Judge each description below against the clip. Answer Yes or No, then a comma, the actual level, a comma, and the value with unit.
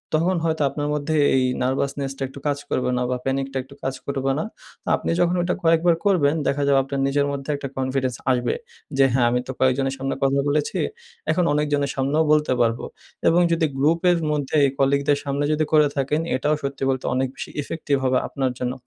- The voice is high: No, medium, 140 Hz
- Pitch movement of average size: No, narrow, 2.2 semitones